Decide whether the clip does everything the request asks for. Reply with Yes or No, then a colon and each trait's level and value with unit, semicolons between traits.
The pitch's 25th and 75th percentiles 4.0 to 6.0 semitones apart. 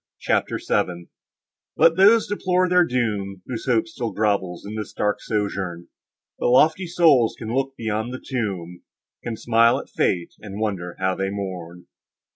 Yes: average, 5.2 semitones